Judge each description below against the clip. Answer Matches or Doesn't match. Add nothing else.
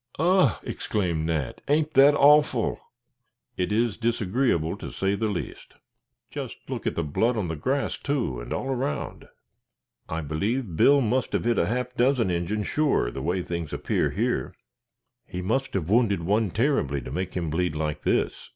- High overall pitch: Doesn't match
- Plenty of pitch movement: Matches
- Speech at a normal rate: Matches